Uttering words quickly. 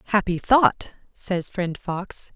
No: slow, 125 wpm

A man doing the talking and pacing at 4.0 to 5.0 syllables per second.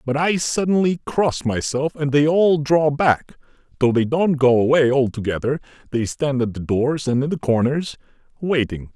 Yes: male; 4.6 syllables/s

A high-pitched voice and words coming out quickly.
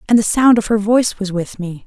Yes: high, 210 Hz; fast, 290 wpm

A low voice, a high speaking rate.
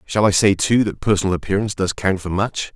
Yes: low, 100 Hz; fast, 240 wpm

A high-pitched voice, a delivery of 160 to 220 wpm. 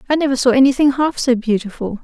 Yes: very high, 255 Hz; fast, 205 wpm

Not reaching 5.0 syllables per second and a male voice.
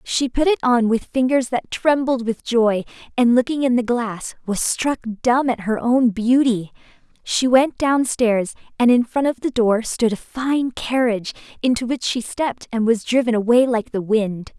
No: 4.5 syllables/s; female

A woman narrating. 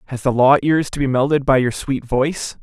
No: male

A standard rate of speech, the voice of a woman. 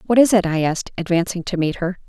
No: fast, 260 wpm; female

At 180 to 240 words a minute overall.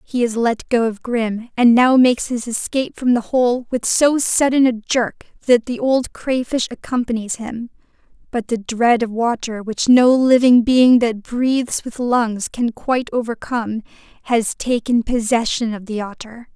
No: average, 170 wpm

